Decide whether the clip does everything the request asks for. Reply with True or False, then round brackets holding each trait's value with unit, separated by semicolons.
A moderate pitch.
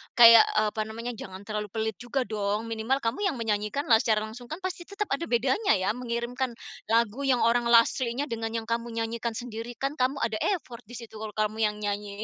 False (230 Hz)